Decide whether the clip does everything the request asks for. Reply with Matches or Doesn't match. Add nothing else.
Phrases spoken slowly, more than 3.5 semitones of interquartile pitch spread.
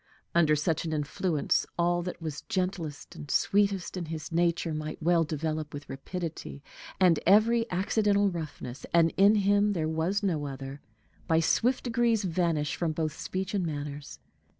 Doesn't match